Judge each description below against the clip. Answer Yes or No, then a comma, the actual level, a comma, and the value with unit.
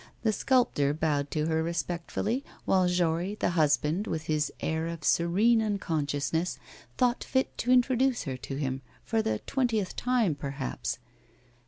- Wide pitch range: Yes, wide, 6.8 semitones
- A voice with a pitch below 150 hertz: No, medium, 170 Hz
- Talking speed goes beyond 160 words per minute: No, average, 145 wpm